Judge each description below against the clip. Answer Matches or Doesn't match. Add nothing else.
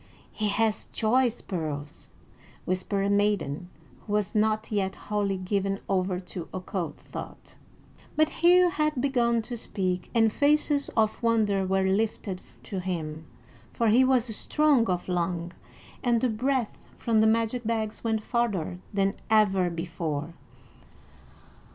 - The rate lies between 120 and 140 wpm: Matches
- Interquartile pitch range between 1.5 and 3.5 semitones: Doesn't match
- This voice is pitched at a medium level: Doesn't match